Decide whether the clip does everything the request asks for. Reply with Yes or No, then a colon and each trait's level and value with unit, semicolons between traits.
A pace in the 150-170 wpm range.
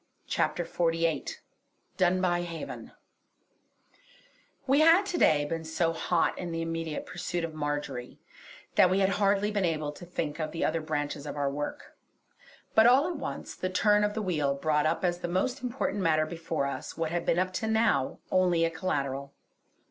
No: average, 180 wpm